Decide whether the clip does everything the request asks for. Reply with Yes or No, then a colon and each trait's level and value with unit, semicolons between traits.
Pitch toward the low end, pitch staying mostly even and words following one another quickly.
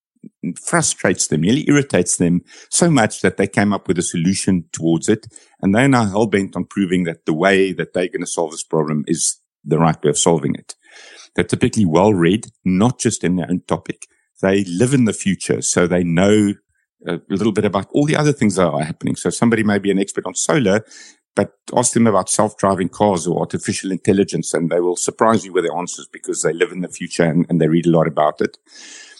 No: low, 100 Hz; average, 4.8 semitones; fast, 220 wpm